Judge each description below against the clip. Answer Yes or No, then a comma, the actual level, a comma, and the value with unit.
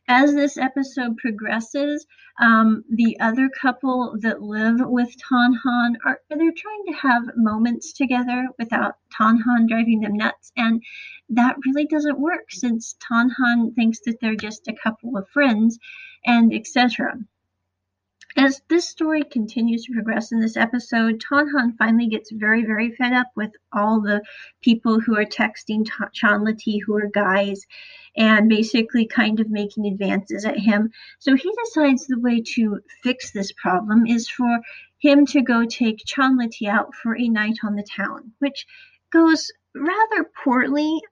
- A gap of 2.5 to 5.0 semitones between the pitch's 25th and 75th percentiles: Yes, average, 3.7 semitones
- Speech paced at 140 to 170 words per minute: Yes, average, 155 wpm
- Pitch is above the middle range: Yes, high, 235 Hz